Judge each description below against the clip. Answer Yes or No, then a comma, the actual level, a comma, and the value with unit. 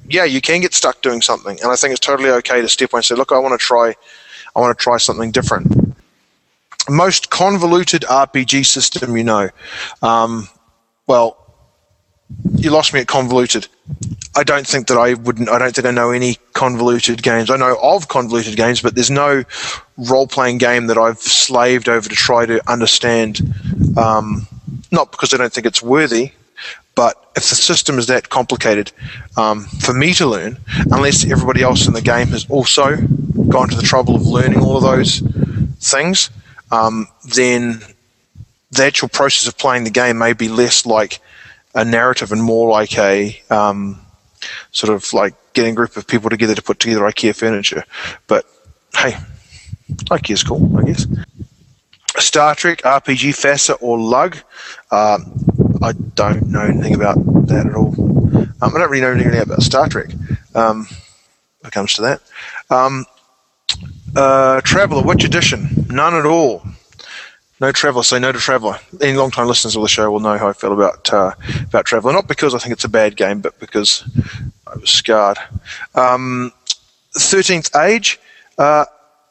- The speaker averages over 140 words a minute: Yes, average, 175 wpm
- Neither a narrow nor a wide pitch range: Yes, average, 3.0 semitones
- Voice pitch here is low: Yes, low, 120 Hz